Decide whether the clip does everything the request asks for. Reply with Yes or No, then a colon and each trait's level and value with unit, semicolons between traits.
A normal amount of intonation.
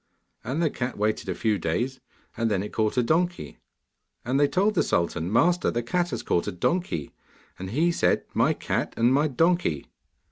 No: wide, 8.1 semitones